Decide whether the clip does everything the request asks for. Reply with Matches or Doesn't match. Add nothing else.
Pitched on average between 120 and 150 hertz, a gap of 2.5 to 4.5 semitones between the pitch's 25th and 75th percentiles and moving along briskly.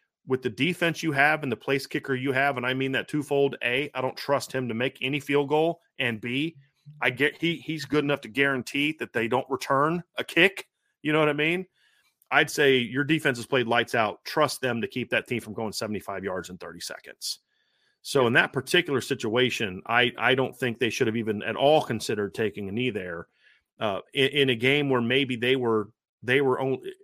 Matches